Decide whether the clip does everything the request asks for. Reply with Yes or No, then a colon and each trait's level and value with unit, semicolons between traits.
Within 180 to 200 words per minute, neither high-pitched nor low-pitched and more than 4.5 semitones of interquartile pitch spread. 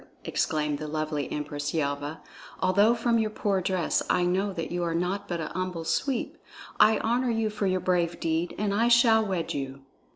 Yes: average, 190 wpm; medium, 180 Hz; average, 4.9 semitones